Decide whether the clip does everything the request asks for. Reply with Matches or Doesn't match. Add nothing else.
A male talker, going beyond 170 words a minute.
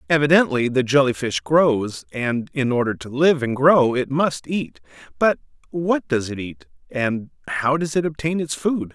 Matches